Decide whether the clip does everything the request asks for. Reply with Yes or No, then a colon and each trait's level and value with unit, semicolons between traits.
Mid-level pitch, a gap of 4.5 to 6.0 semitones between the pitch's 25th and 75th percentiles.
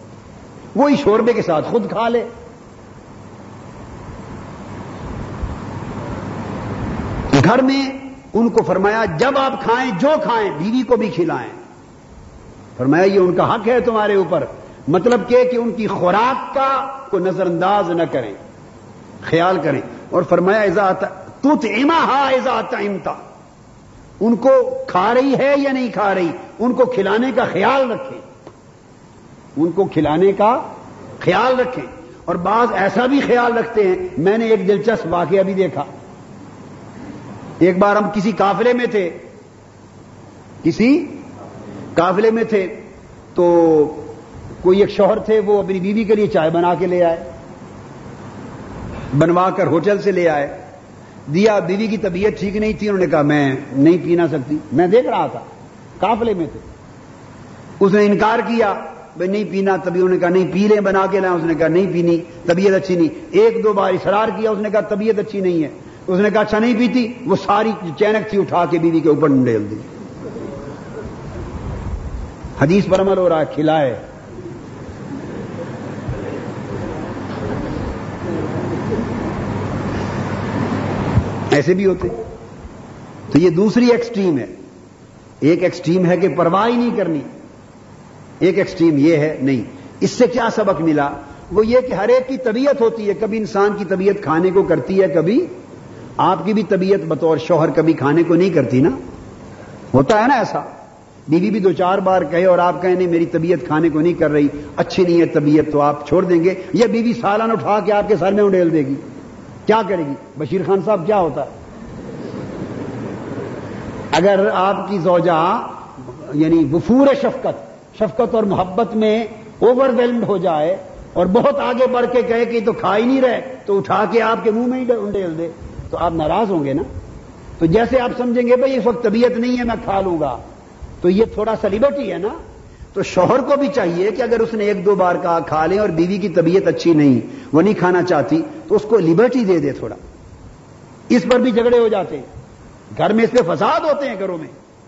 No: high, 195 Hz; average, 5.1 semitones